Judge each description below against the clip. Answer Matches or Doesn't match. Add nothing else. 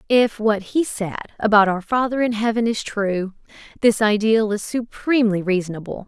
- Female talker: Matches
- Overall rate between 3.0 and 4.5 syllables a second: Doesn't match